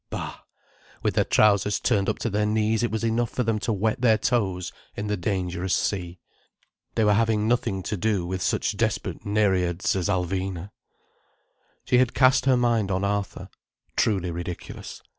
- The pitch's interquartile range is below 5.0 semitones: Yes, average, 3.1 semitones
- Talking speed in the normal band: Yes, average, 170 wpm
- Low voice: Yes, low, 105 Hz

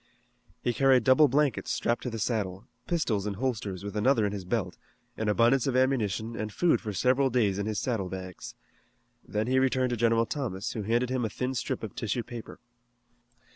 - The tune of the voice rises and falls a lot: No, average, 3.8 semitones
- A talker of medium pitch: No, low, 115 Hz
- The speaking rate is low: No, average, 195 wpm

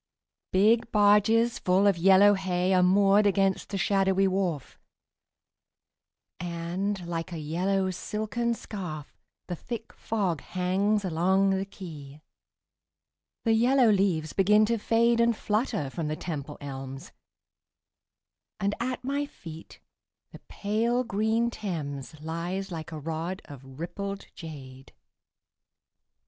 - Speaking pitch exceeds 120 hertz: Yes, high, 190 Hz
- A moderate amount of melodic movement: Yes, average, 4.2 semitones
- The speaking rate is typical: No, slow, 120 wpm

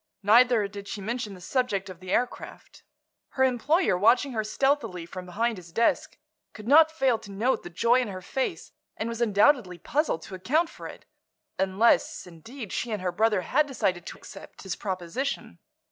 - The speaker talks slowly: No, average, 175 wpm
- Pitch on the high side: Yes, high, 220 Hz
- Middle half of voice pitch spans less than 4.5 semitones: No, average, 5.3 semitones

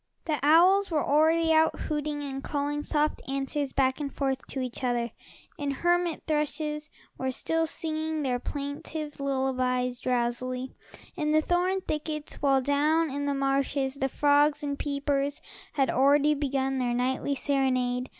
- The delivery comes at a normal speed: Yes, average, 150 wpm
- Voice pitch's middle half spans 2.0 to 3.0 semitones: Yes, narrow, 2.4 semitones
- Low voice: No, very high, 285 Hz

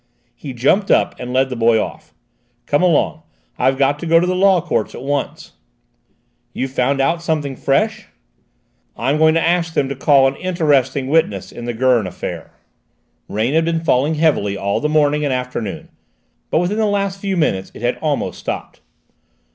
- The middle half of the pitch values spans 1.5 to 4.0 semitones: No, average, 4.5 semitones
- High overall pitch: No, medium, 145 Hz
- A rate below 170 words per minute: No, average, 180 wpm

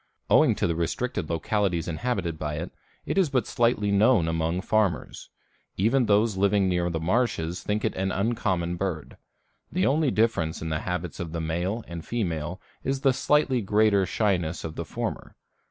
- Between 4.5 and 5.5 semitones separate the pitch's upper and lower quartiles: Yes, average, 4.8 semitones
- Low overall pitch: Yes, very low, 95 Hz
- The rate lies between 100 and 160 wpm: No, average, 170 wpm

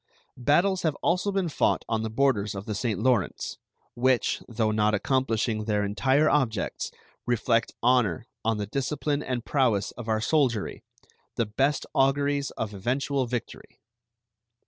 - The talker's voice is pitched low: Yes, low, 120 Hz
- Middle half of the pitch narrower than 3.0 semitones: No, average, 4.3 semitones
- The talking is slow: No, average, 145 wpm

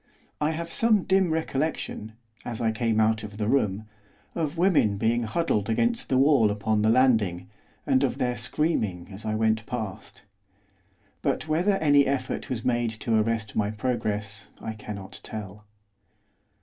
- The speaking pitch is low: Yes, low, 115 Hz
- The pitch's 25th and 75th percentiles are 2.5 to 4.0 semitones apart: No, average, 4.8 semitones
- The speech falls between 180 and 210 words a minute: No, average, 155 wpm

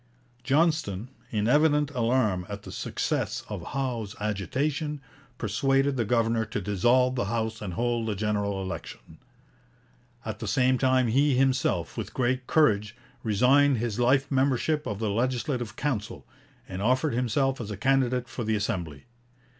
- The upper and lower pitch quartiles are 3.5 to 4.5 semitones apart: Yes, average, 4.1 semitones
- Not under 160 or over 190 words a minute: No, average, 145 wpm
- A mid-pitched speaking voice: No, low, 120 Hz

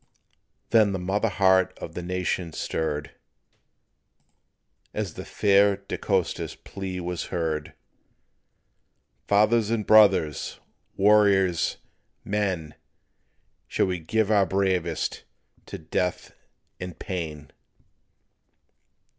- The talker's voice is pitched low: Yes, very low, 95 Hz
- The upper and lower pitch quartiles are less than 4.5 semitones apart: Yes, average, 2.9 semitones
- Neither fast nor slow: No, slow, 95 wpm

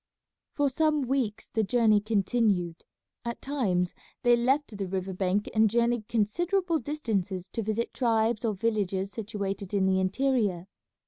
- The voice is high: Yes, high, 220 Hz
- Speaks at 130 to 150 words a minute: Yes, average, 140 wpm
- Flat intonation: No, average, 3.8 semitones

